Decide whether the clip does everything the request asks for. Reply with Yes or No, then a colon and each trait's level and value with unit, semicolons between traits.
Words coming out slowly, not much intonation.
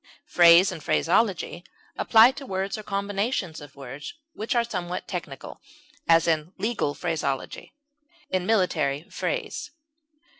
No: slow, 120 wpm; average, 5.2 semitones